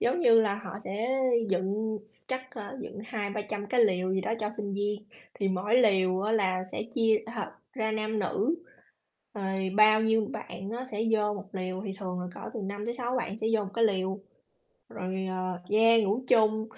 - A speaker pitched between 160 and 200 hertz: No, high, 210 Hz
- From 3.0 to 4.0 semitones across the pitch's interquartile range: No, narrow, 2.5 semitones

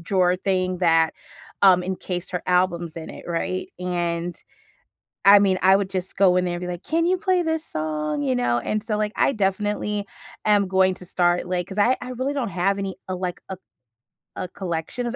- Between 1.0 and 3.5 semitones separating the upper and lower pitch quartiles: Yes, narrow, 2.5 semitones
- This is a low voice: No, medium, 185 Hz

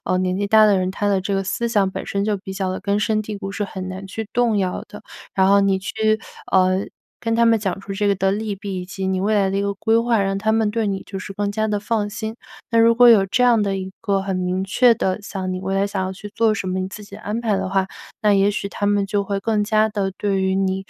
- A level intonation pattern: Yes, narrow, 1.9 semitones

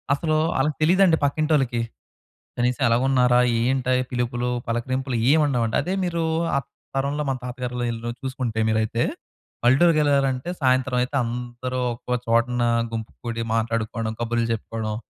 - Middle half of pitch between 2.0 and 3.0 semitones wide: Yes, narrow, 2.6 semitones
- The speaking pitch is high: No, low, 125 Hz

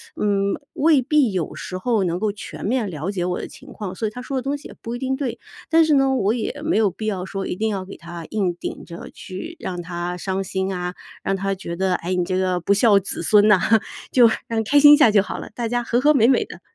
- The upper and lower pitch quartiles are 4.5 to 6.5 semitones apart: Yes, average, 5.0 semitones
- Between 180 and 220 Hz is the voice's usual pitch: Yes, high, 205 Hz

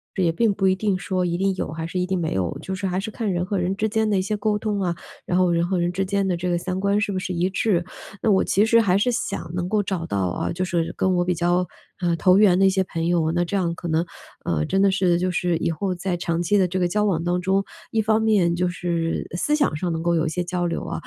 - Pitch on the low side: No, medium, 185 Hz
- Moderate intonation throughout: No, narrow, 2.3 semitones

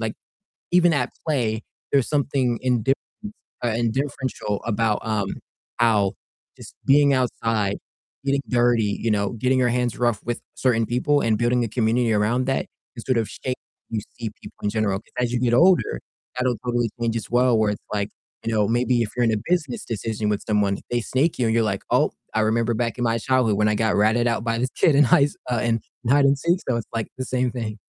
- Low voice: Yes, low, 120 Hz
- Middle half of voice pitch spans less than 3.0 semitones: Yes, narrow, 2.5 semitones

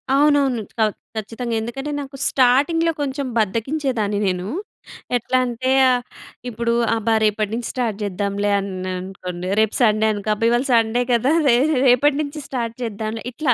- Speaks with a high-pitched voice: Yes, high, 230 Hz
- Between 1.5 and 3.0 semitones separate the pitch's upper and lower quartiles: No, average, 3.7 semitones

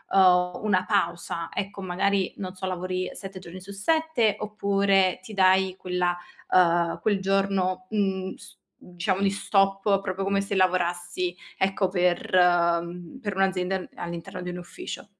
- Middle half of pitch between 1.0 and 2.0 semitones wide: Yes, narrow, 1.7 semitones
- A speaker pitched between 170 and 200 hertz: Yes, medium, 185 Hz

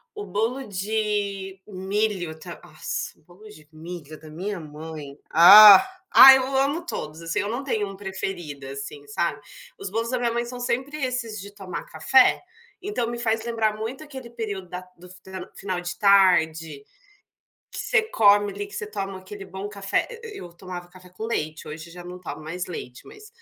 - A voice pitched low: No, high, 195 Hz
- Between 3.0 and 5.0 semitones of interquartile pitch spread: Yes, average, 4.4 semitones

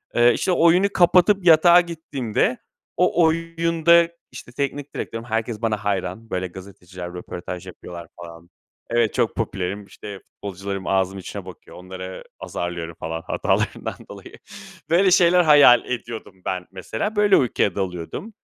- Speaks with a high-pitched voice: No, low, 110 Hz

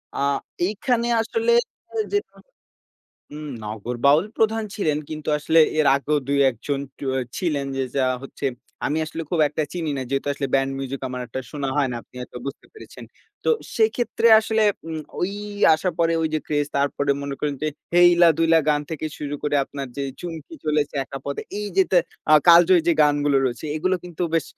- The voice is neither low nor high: Yes, medium, 150 Hz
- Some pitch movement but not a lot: Yes, average, 3.7 semitones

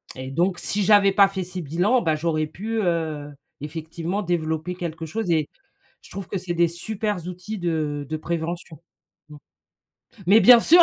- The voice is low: No, medium, 175 Hz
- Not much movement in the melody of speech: No, average, 3.7 semitones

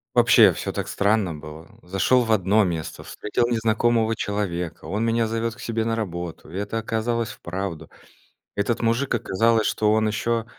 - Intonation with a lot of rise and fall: No, average, 3.1 semitones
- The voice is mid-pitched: No, low, 110 Hz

